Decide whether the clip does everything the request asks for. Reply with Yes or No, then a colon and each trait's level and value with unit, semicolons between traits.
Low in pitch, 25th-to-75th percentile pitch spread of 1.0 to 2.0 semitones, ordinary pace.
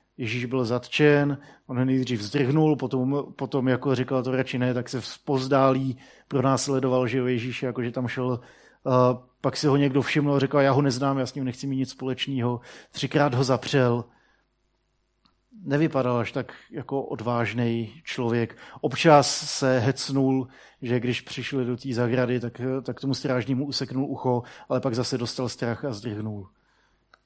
Yes: low, 130 Hz; narrow, 1.7 semitones; average, 160 wpm